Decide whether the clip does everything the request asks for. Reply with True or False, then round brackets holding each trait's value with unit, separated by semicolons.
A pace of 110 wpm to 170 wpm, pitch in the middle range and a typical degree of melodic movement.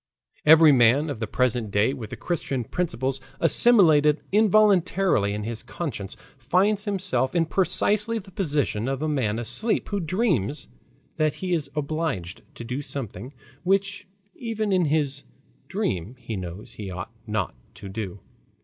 False (150 wpm; 145 Hz; 8.3 semitones)